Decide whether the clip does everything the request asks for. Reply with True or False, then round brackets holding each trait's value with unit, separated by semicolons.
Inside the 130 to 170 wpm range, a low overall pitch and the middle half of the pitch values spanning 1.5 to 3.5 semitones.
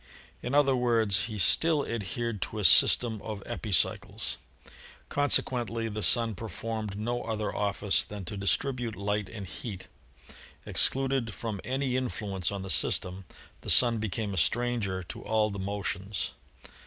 True (140 wpm; 110 Hz; 3.1 semitones)